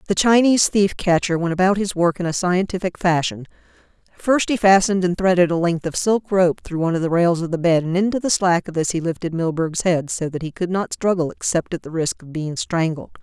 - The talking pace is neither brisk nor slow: No, fast, 240 wpm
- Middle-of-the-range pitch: Yes, medium, 175 Hz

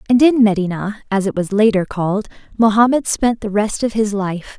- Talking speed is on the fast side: No, average, 195 wpm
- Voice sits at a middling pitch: No, high, 210 Hz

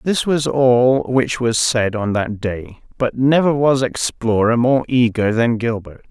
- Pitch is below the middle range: Yes, low, 120 Hz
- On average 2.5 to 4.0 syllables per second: Yes, 3.9 syllables/s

